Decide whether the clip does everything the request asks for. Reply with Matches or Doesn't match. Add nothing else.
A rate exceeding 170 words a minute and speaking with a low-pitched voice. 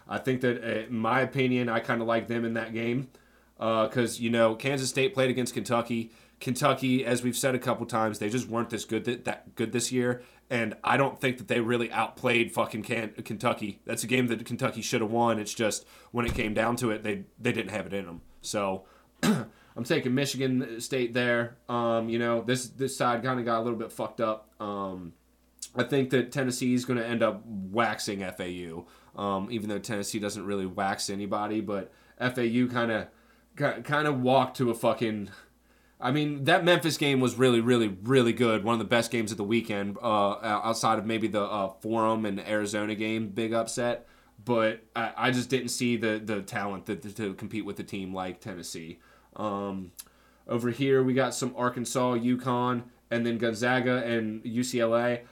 Matches